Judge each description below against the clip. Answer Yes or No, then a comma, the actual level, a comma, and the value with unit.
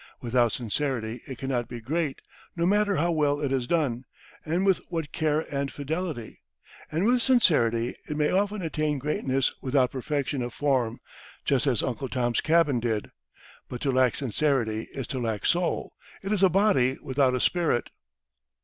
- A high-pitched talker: No, medium, 140 Hz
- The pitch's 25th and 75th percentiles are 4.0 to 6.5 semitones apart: Yes, average, 4.8 semitones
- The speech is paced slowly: No, average, 165 wpm